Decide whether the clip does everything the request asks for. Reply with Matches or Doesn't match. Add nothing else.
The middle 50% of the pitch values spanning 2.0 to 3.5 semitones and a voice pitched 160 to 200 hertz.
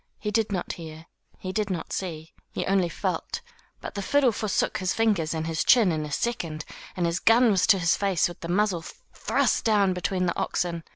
Doesn't match